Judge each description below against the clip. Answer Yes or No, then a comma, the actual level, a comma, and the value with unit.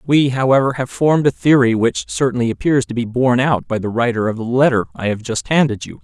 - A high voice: No, low, 125 Hz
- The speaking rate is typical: No, fast, 240 wpm